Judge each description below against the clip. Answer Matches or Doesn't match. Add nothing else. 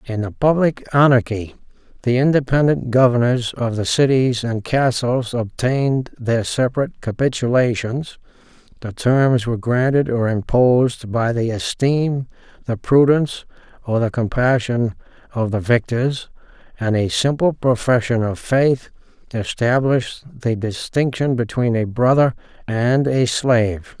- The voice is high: Doesn't match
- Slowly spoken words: Matches